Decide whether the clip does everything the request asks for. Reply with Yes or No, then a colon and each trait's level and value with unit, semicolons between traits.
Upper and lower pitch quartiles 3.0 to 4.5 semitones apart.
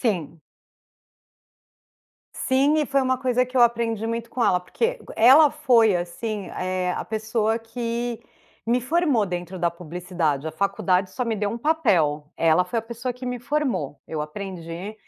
No: wide, 5.6 semitones